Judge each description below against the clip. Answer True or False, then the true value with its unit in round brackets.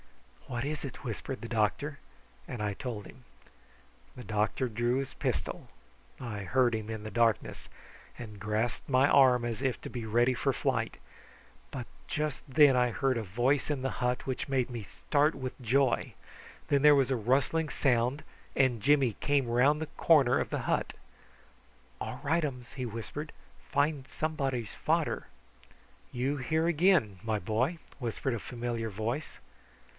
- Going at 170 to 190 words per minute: False (160 wpm)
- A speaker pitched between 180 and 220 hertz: False (125 Hz)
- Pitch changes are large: False (3.4 semitones)